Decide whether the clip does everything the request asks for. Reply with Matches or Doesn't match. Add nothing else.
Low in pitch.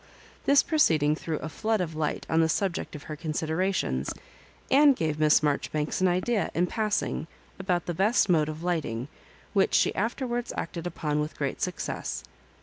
Doesn't match